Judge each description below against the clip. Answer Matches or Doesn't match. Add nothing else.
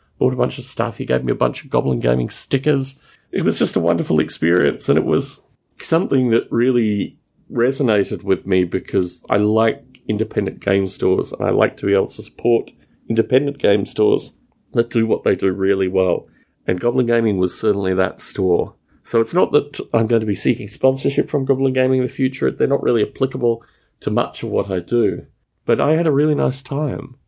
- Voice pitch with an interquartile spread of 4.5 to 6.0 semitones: Matches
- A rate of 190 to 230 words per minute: Matches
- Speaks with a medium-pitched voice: Doesn't match